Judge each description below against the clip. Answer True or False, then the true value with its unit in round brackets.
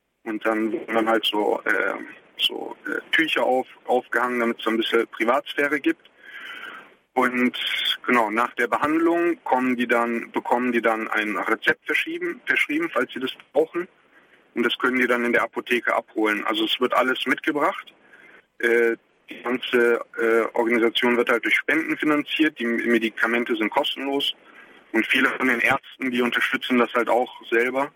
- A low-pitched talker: True (120 Hz)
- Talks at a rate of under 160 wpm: False (165 wpm)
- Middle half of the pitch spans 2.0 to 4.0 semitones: True (3.4 semitones)